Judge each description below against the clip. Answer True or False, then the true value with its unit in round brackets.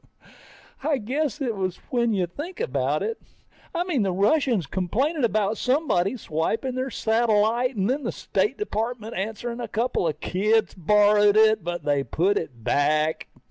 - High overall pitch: True (215 Hz)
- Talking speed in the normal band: True (160 wpm)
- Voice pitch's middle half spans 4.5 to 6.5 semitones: True (5.5 semitones)